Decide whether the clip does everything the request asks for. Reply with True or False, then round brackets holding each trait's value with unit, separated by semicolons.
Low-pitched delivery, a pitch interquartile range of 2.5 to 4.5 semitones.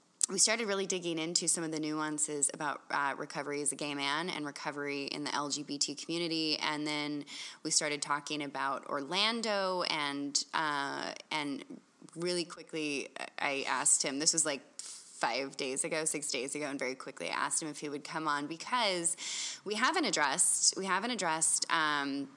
False (155 Hz; 2.8 semitones)